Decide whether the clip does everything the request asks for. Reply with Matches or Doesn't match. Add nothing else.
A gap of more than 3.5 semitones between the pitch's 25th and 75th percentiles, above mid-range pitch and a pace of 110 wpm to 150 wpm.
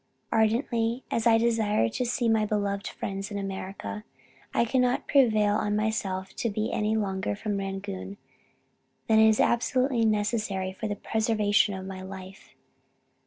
Doesn't match